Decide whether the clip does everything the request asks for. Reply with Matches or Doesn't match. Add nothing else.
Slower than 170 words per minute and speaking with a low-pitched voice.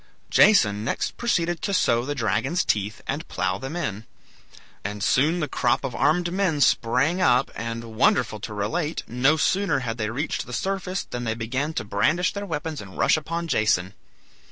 Doesn't match